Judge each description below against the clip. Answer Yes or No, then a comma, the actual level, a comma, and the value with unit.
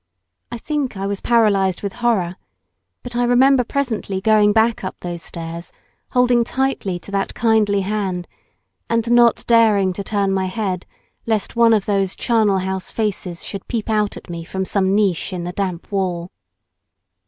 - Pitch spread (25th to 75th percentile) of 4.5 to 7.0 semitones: No, average, 3.5 semitones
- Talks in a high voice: Yes, high, 200 Hz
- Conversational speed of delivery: Yes, average, 165 wpm